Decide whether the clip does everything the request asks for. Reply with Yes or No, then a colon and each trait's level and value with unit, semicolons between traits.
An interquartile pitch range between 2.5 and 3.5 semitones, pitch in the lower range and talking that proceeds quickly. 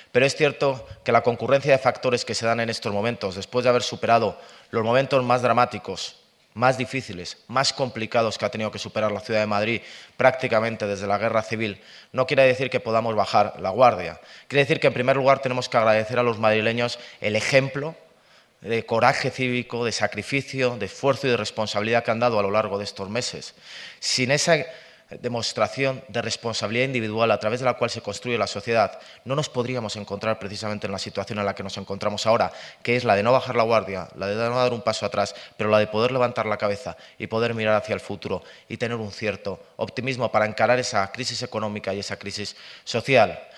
Yes: average, 3.1 semitones; low, 115 Hz; fast, 210 wpm